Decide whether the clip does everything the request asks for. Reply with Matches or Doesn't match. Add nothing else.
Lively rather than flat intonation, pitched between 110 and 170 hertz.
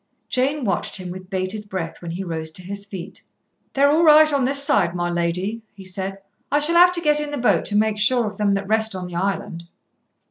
Doesn't match